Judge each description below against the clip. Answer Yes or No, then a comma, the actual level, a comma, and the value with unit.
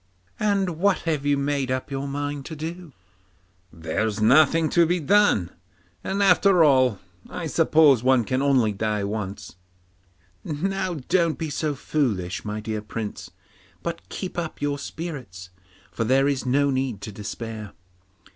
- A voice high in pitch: No, medium, 140 Hz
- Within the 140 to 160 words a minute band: Yes, average, 145 wpm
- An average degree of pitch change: No, wide, 6.6 semitones